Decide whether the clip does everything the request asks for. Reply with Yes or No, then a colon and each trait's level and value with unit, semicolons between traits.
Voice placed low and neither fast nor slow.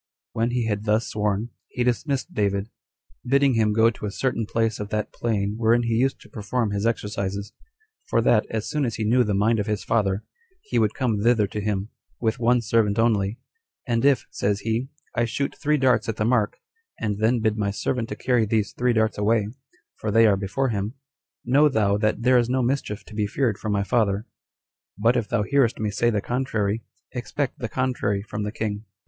No: low, 110 Hz; fast, 210 wpm